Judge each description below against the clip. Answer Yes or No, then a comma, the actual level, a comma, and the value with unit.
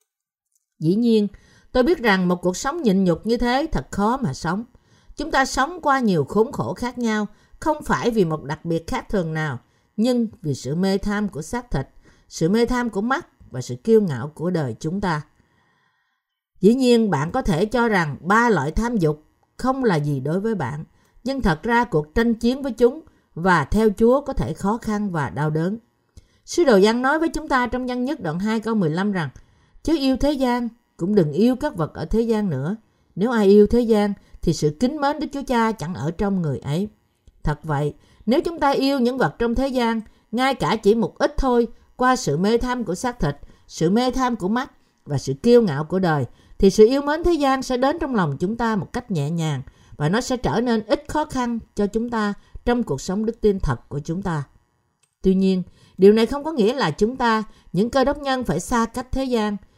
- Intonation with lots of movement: Yes, wide, 6.4 semitones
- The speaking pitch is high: Yes, high, 215 Hz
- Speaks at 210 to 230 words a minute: Yes, average, 225 wpm